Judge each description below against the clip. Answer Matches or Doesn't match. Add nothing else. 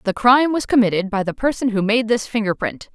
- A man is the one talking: Doesn't match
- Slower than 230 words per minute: Doesn't match